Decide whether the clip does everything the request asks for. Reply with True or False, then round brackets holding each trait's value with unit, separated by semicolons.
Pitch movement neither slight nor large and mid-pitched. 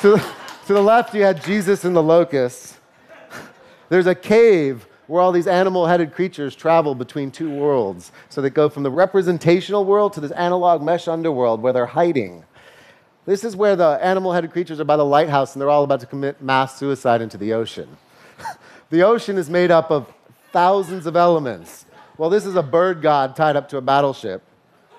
True (4.8 semitones; 165 Hz)